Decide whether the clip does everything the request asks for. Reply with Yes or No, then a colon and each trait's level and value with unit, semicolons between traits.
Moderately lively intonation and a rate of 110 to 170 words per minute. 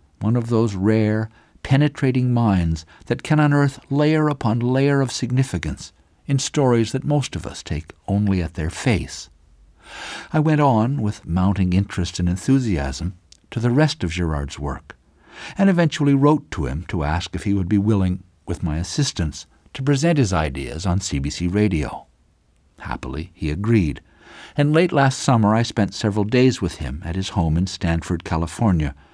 No: wide, 7.9 semitones; average, 165 wpm